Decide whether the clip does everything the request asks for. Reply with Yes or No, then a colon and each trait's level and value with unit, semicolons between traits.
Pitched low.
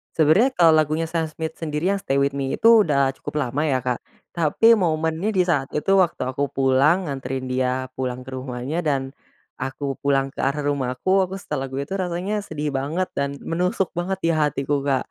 No: medium, 150 Hz